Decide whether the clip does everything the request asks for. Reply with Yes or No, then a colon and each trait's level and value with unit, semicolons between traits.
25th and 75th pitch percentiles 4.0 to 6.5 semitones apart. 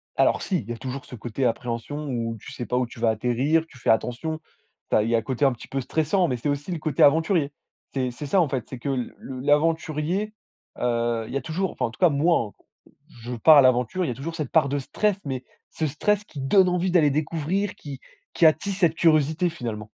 Yes: average, 4.9 semitones